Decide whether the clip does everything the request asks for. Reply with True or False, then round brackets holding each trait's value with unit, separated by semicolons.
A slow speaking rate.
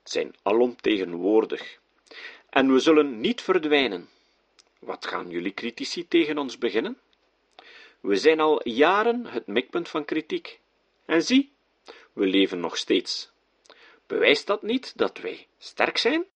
True (130 wpm)